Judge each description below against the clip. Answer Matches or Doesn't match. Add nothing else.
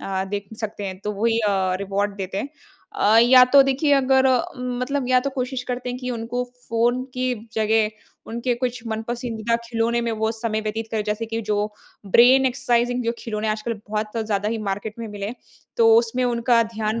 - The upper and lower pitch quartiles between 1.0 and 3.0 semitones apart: Matches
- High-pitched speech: Matches